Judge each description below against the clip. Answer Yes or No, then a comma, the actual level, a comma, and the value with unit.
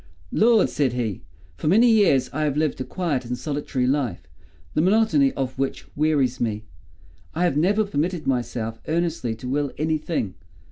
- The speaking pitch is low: No, medium, 145 Hz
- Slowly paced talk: No, average, 170 wpm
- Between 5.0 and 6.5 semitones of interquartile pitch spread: Yes, wide, 5.5 semitones